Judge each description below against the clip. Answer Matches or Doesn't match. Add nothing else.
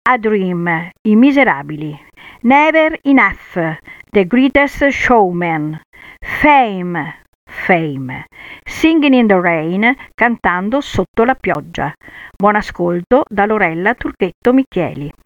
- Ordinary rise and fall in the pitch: Doesn't match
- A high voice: Matches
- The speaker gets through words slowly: Matches